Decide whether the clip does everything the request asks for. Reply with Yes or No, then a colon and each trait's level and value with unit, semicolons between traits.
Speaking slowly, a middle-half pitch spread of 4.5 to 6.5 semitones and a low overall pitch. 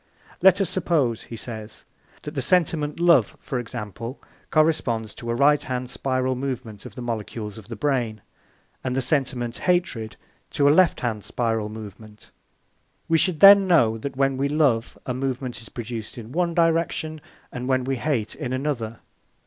No: average, 170 wpm; average, 4.9 semitones; low, 130 Hz